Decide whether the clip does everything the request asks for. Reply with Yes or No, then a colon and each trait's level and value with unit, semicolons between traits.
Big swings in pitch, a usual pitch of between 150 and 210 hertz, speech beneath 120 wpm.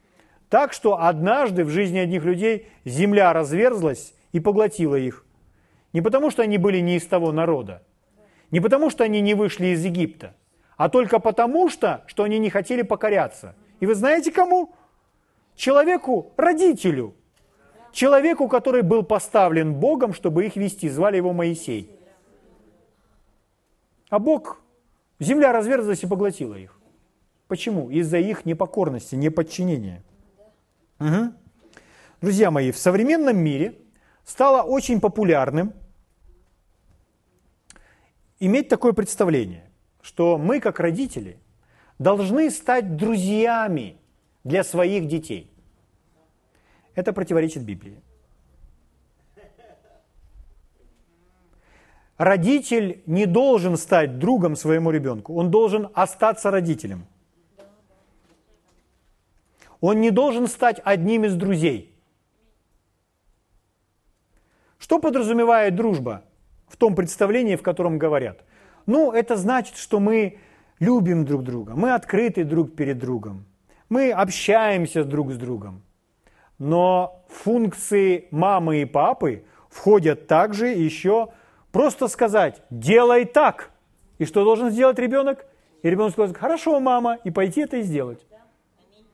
Yes: wide, 7.4 semitones; high, 190 Hz; slow, 110 wpm